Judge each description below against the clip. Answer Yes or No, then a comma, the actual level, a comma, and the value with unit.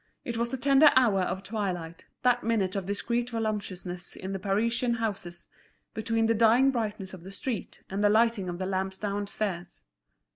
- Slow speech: No, average, 175 wpm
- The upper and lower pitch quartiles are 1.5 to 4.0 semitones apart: Yes, average, 3.4 semitones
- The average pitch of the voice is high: Yes, high, 210 Hz